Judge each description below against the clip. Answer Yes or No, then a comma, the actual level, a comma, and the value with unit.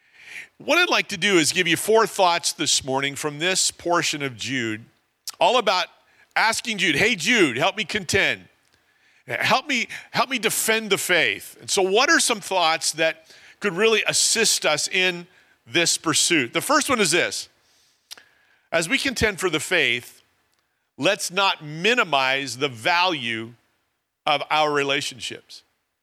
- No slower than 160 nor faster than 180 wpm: No, average, 150 wpm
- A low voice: No, medium, 180 Hz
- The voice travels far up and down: Yes, wide, 7.3 semitones